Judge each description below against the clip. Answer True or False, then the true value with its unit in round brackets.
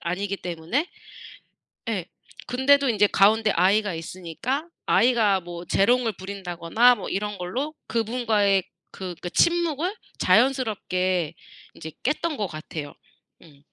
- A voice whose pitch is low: False (200 Hz)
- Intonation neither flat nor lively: False (5.7 semitones)